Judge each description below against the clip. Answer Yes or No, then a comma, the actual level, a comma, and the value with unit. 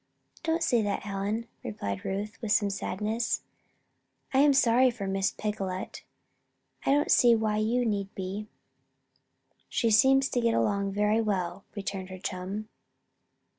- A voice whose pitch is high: Yes, high, 210 Hz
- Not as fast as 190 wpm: Yes, average, 140 wpm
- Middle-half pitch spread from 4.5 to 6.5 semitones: No, average, 3.1 semitones